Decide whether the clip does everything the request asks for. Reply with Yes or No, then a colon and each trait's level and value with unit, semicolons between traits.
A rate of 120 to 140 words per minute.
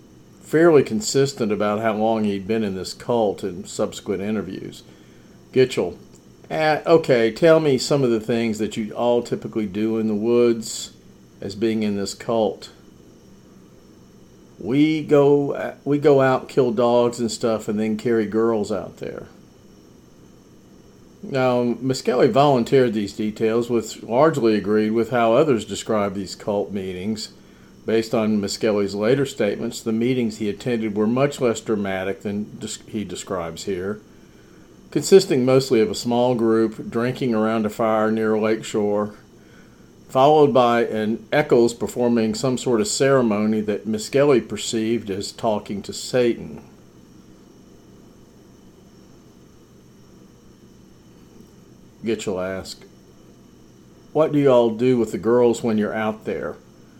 Yes: slow, 135 wpm